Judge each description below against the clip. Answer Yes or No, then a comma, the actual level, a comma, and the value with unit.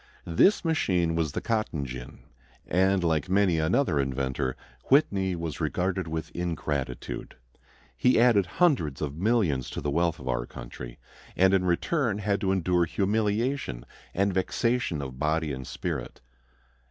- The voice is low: Yes, very low, 90 Hz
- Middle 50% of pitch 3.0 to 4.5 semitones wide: No, wide, 5.5 semitones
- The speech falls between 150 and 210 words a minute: No, average, 140 wpm